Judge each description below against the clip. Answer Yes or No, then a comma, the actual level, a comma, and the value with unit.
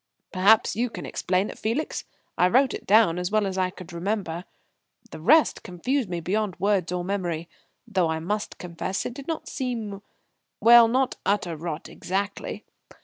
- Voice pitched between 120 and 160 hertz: No, high, 200 Hz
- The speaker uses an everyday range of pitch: Yes, average, 4.0 semitones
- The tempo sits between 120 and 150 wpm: No, average, 170 wpm